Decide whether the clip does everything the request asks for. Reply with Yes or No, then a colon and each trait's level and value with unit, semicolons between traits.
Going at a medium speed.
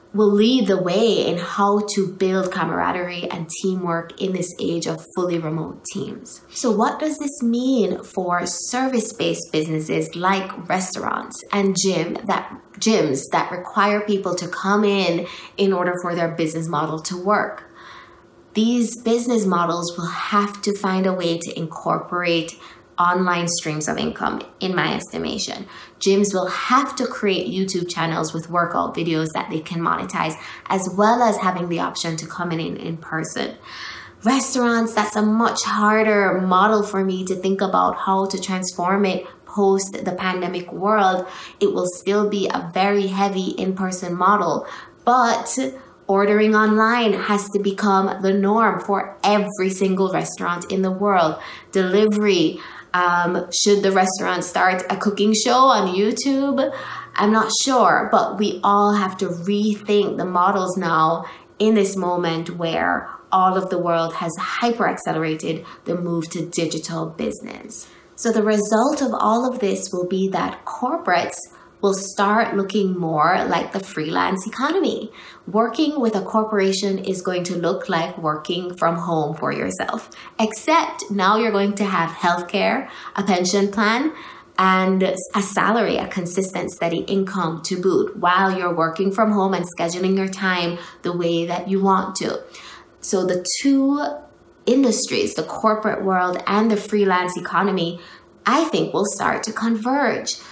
Yes: average, 155 wpm